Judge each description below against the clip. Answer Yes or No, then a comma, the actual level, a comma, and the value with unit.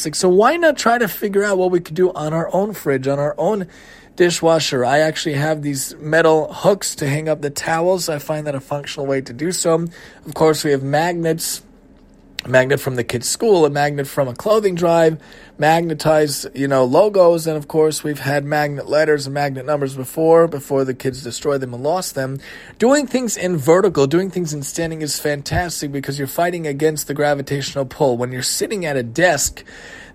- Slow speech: No, fast, 205 wpm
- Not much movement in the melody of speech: No, average, 3.2 semitones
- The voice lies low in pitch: No, medium, 150 Hz